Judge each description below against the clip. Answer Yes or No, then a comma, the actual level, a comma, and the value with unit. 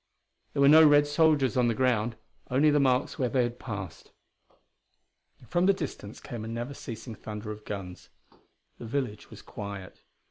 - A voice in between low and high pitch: No, low, 120 Hz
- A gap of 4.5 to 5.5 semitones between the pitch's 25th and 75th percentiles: Yes, average, 4.9 semitones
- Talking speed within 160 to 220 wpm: Yes, average, 170 wpm